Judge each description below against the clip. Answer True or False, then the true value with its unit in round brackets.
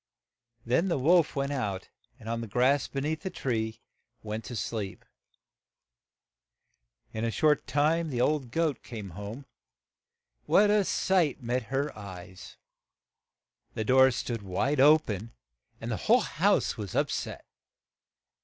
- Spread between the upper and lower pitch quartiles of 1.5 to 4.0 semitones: False (5.2 semitones)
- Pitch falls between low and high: False (125 Hz)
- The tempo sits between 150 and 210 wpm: False (140 wpm)